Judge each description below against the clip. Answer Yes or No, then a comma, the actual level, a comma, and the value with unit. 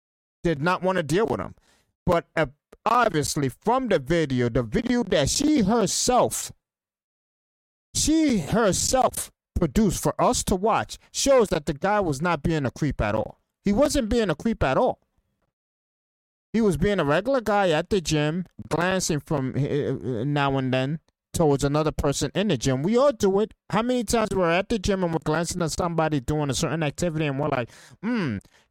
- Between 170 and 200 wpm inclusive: Yes, average, 180 wpm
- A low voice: No, medium, 170 Hz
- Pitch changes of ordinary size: No, wide, 6.2 semitones